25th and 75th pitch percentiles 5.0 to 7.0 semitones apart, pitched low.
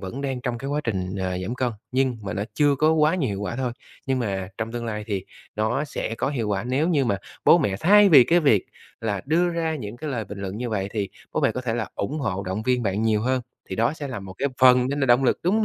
Yes: average, 5.3 semitones; low, 120 Hz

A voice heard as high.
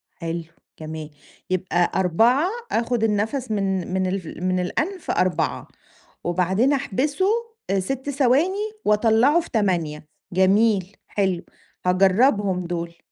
Yes: high, 195 Hz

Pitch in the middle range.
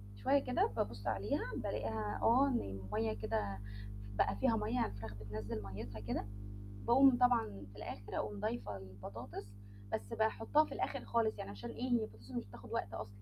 No: low, 110 Hz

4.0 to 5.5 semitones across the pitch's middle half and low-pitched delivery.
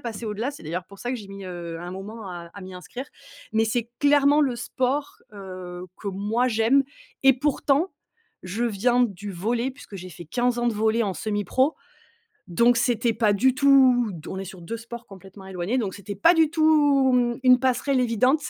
No: average, 4.7 semitones; high, 230 Hz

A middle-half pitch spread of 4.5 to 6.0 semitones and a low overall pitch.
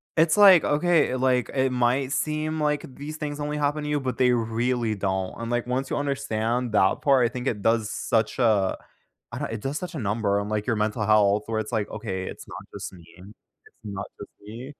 Yes: average, 5.0 semitones; low, 120 Hz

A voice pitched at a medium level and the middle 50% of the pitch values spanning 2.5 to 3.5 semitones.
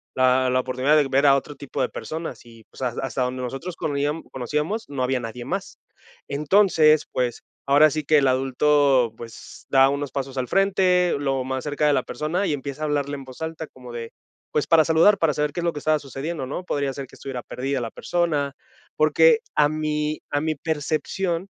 Yes: medium, 145 Hz; average, 2.9 semitones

